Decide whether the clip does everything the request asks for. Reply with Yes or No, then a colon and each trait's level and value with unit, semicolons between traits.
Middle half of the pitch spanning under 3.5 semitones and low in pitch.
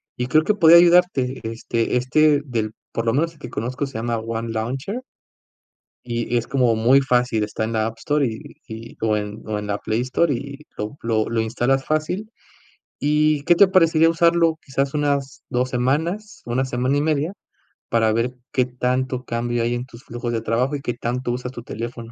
No: average, 4.1 semitones; low, 125 Hz